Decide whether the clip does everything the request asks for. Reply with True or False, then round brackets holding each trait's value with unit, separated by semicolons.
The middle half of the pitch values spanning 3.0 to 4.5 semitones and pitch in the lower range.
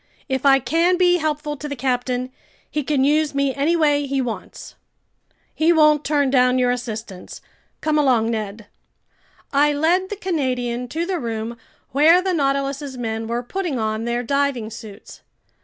False (3.9 semitones; 275 Hz)